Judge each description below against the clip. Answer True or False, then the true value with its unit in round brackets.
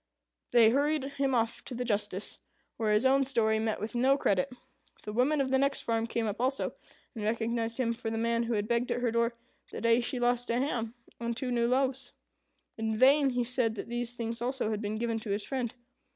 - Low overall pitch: False (235 Hz)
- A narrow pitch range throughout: True (2.2 semitones)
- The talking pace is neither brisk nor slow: False (225 wpm)